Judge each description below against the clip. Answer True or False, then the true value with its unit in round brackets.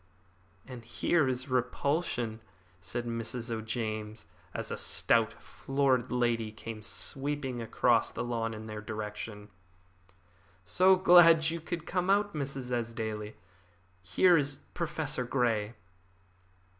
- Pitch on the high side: False (120 Hz)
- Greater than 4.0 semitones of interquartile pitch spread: True (4.7 semitones)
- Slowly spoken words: True (115 wpm)